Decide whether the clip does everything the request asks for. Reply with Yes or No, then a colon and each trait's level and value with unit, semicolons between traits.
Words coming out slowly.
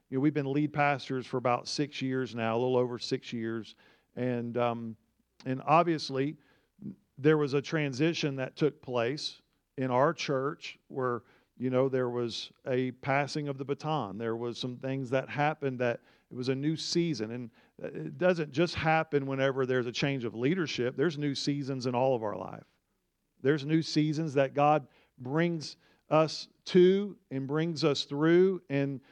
No: average, 175 wpm